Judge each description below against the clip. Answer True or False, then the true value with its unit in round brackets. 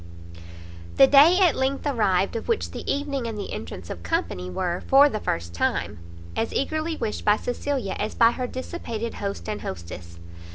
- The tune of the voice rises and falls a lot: True (7.6 semitones)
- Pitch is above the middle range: True (230 Hz)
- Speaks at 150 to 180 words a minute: True (175 wpm)